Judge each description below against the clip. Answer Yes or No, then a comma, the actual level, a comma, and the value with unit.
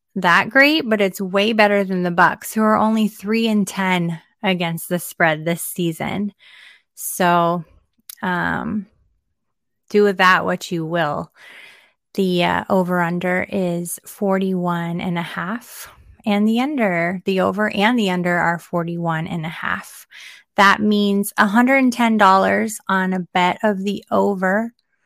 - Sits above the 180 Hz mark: Yes, high, 190 Hz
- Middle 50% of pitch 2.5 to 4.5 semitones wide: Yes, average, 3.1 semitones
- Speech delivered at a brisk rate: No, average, 145 wpm